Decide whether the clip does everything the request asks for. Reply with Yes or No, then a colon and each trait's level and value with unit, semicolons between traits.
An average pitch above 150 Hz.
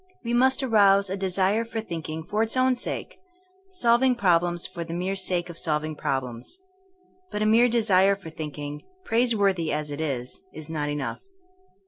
Yes: medium, 185 Hz